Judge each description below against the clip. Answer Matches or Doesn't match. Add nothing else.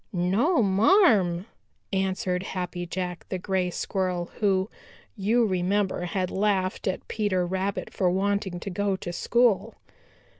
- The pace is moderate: Doesn't match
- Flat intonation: Matches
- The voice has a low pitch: Doesn't match